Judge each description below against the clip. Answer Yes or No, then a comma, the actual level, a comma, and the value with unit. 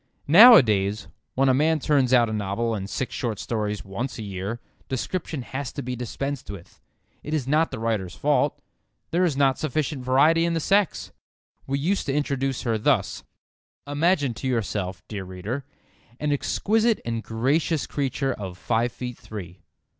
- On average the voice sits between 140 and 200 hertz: No, low, 130 Hz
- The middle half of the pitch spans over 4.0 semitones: Yes, average, 5.2 semitones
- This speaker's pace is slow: No, average, 165 wpm